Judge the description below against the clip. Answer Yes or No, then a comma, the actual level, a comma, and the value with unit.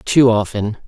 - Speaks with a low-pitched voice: Yes, low, 110 Hz